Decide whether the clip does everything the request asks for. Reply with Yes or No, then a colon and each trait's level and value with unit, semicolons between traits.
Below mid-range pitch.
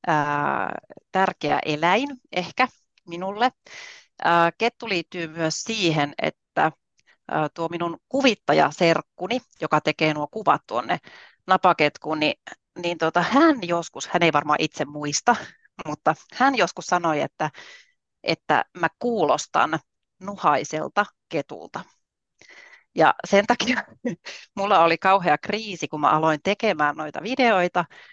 No: medium, 175 Hz